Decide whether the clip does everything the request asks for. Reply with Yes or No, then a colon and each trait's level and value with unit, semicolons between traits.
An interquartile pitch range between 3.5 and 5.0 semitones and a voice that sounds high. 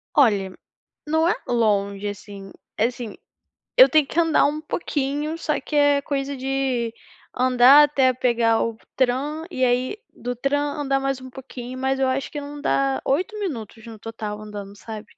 Yes: average, 4.0 semitones; very high, 260 Hz